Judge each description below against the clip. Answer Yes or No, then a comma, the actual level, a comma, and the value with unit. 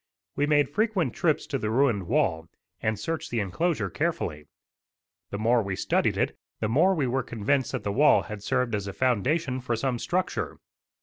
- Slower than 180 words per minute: No, average, 185 wpm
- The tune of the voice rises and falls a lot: Yes, wide, 6.0 semitones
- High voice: No, low, 125 Hz